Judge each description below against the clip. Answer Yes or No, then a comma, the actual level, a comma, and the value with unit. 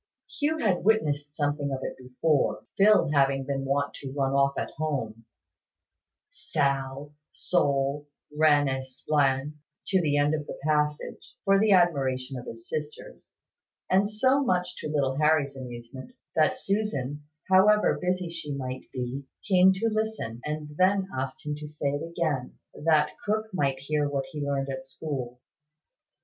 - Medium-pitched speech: Yes, medium, 145 Hz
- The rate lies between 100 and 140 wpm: No, average, 155 wpm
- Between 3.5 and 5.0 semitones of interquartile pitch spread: Yes, average, 4.6 semitones